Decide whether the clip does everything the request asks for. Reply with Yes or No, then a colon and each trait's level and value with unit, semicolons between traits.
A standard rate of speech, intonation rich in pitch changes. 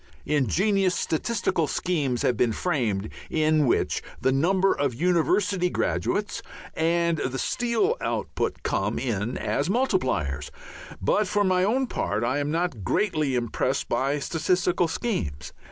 No: slow, 130 wpm; wide, 6.5 semitones